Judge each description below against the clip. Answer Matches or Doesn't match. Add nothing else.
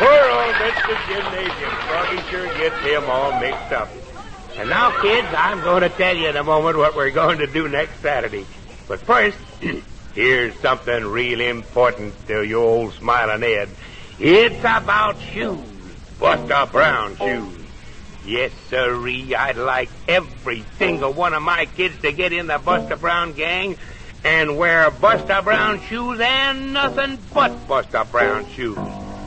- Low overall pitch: Doesn't match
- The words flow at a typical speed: Matches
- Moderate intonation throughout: Doesn't match